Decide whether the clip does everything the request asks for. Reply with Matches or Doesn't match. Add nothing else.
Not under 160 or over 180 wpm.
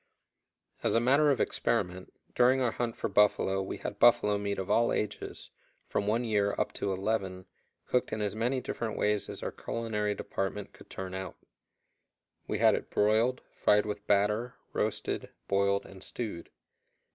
Matches